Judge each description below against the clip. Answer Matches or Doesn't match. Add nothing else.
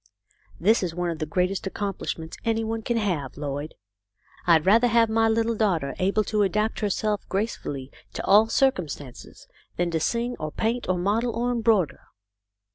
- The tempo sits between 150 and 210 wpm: Matches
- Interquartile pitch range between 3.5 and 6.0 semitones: Matches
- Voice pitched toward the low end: Doesn't match